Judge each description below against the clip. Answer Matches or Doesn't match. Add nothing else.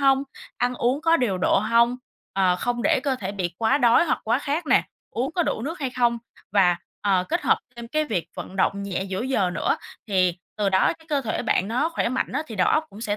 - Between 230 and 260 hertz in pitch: Matches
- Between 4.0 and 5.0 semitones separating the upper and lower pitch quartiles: Doesn't match